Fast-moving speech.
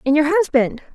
No: average, 190 wpm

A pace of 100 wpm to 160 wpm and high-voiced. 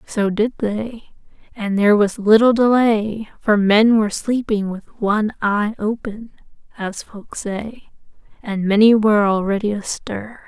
Yes: average, 140 wpm; high, 215 Hz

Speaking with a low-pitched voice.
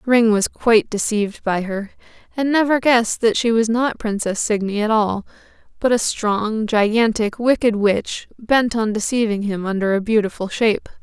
No: high, 220 Hz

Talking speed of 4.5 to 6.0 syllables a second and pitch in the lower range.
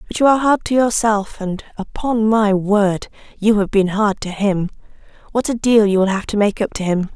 No: 5.1 syllables/s; high, 210 Hz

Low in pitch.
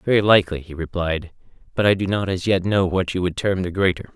Yes: very low, 95 Hz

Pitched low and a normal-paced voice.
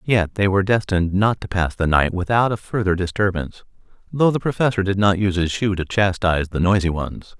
No: very low, 95 Hz; fast, 210 wpm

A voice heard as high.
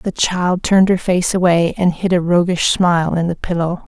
No: medium, 175 Hz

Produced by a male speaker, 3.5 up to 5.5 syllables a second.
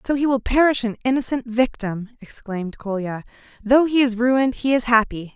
No: female; 5.4 syllables/s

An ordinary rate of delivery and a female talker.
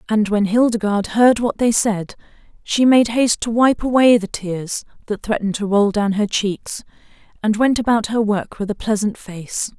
Yes: average, 190 wpm; female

